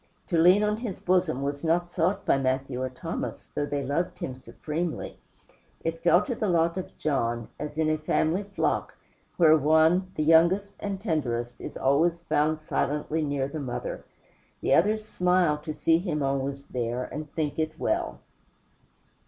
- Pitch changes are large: No, average, 3.8 semitones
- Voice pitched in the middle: Yes, medium, 155 Hz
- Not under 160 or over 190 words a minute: Yes, average, 170 wpm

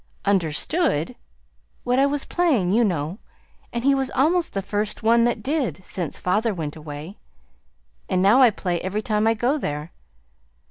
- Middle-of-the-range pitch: No, high, 215 Hz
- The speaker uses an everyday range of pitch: No, wide, 6.0 semitones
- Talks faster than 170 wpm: No, average, 165 wpm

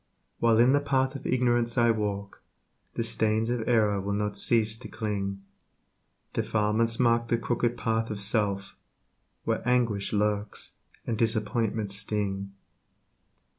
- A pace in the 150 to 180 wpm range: No, slow, 135 wpm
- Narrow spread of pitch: Yes, narrow, 2.2 semitones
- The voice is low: Yes, low, 110 Hz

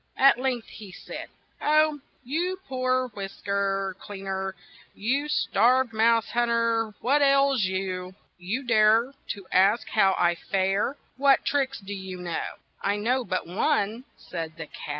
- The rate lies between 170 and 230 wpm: No, average, 160 wpm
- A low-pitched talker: No, high, 220 Hz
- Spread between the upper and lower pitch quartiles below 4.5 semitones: No, average, 5.1 semitones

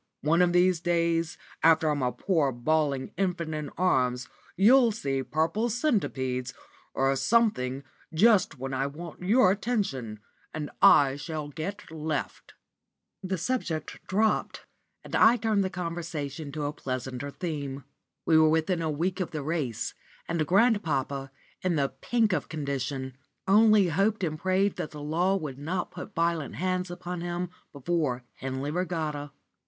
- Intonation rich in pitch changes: No, average, 4.6 semitones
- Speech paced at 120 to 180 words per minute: Yes, average, 150 wpm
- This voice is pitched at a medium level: Yes, medium, 160 Hz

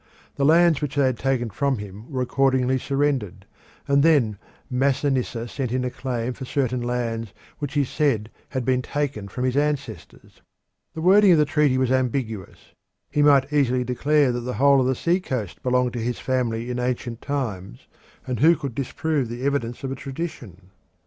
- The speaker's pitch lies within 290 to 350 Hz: No, low, 130 Hz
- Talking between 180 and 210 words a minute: Yes, average, 185 wpm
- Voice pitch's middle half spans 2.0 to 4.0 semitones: Yes, average, 2.8 semitones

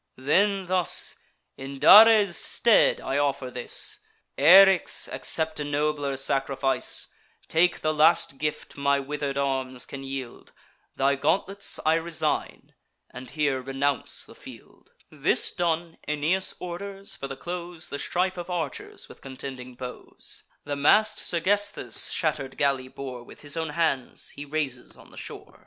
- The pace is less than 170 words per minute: Yes, average, 140 wpm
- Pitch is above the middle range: No, medium, 145 Hz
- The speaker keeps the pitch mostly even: No, average, 4.2 semitones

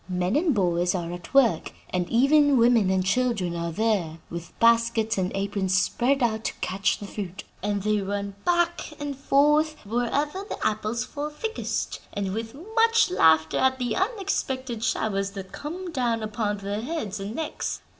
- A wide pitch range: Yes, wide, 6.2 semitones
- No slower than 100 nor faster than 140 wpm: No, average, 165 wpm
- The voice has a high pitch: Yes, high, 225 Hz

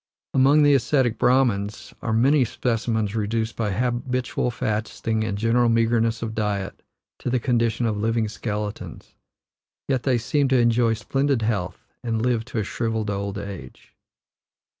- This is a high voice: No, low, 115 Hz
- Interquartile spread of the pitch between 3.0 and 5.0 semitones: No, narrow, 2.4 semitones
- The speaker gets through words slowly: No, average, 145 wpm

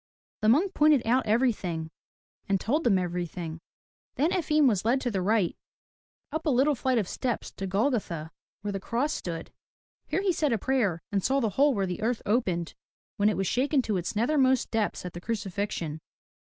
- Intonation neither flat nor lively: No, wide, 6.1 semitones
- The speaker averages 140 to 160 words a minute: No, average, 195 wpm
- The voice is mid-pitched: No, high, 220 Hz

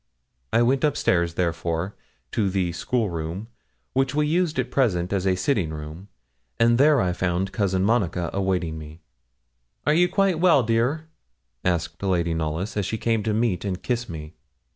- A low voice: Yes, very low, 95 Hz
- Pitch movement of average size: No, wide, 5.9 semitones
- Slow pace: No, average, 170 wpm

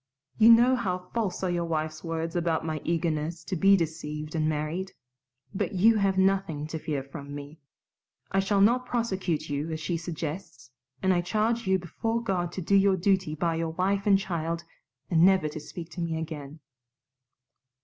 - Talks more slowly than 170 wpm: No, average, 180 wpm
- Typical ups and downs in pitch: Yes, average, 3.6 semitones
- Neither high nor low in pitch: Yes, medium, 170 Hz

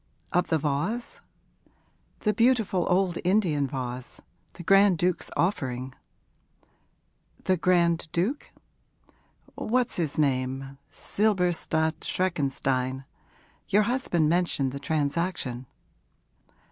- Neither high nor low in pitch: Yes, medium, 170 Hz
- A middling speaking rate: No, slow, 90 wpm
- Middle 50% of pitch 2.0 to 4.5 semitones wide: No, average, 5.3 semitones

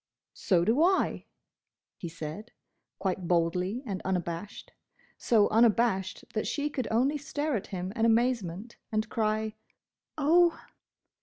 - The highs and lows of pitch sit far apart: No, average, 5.0 semitones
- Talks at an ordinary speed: No, slow, 125 wpm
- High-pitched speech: Yes, high, 215 Hz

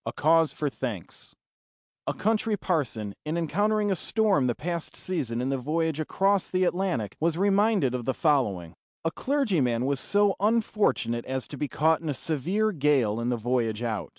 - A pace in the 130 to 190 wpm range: Yes, average, 180 wpm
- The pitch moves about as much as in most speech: No, wide, 7.6 semitones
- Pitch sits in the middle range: Yes, medium, 155 Hz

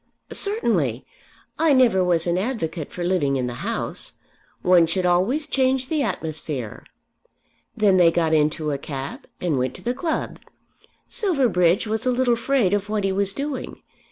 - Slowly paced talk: No, average, 160 wpm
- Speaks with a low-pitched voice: No, high, 190 Hz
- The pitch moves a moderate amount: No, wide, 7.7 semitones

